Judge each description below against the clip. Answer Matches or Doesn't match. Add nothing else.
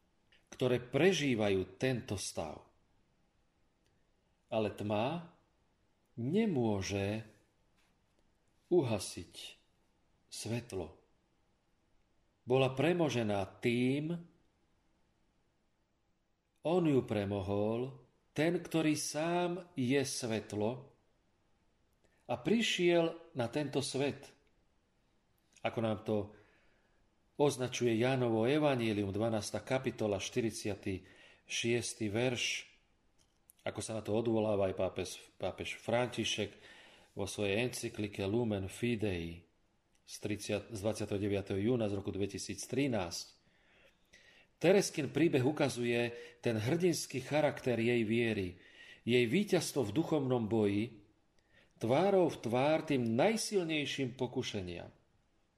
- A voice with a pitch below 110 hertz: Doesn't match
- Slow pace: Matches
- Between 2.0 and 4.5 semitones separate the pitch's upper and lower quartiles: Doesn't match